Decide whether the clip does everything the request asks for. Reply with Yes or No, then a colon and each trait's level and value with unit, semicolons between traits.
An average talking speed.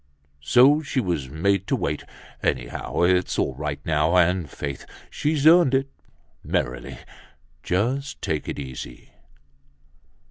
No: slow, 120 wpm